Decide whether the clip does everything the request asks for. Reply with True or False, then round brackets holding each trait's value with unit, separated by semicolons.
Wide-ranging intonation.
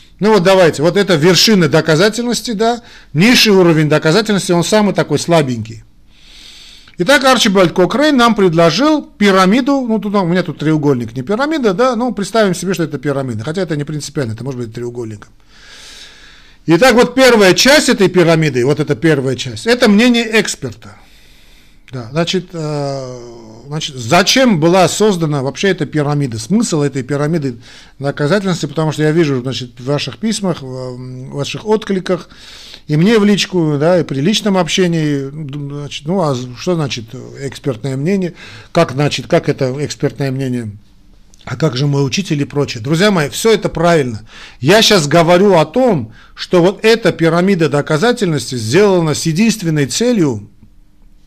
True (6.4 semitones)